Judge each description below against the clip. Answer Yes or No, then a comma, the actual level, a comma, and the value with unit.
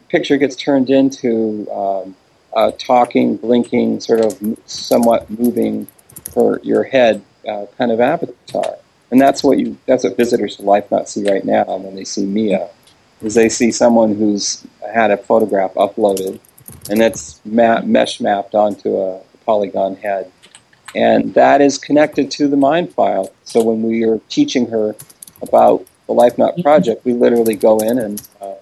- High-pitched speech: No, low, 115 Hz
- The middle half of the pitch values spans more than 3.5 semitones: No, average, 3.0 semitones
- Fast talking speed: No, average, 165 wpm